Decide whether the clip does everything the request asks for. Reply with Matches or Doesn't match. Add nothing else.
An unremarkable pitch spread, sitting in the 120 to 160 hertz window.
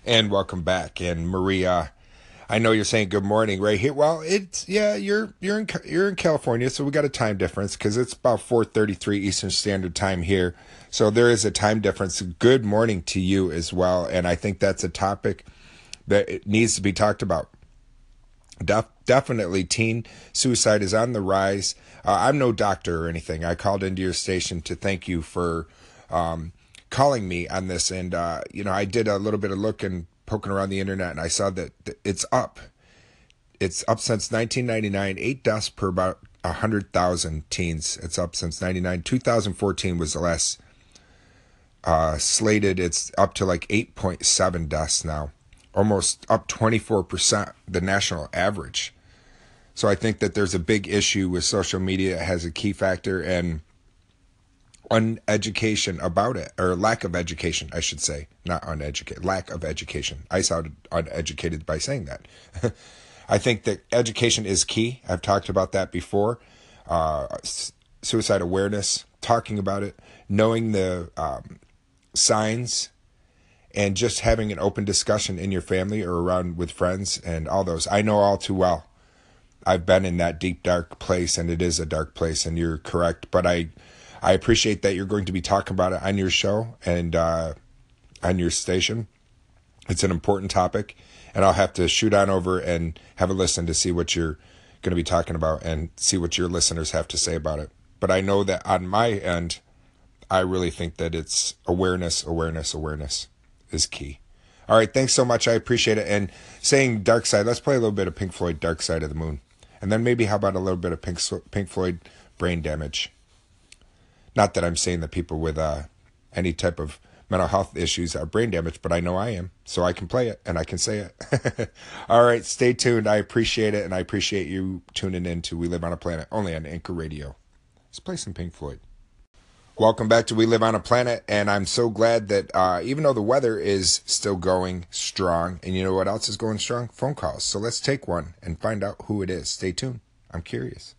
Doesn't match